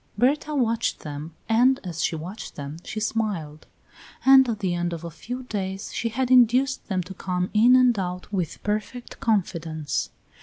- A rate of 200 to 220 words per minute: No, average, 175 wpm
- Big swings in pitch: Yes, wide, 5.9 semitones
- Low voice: No, high, 210 Hz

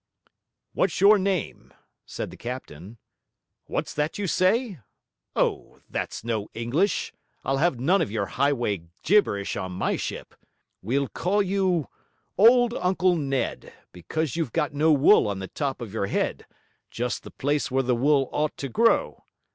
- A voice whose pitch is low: No, medium, 145 Hz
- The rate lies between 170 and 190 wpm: No, average, 155 wpm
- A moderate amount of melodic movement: No, wide, 7.6 semitones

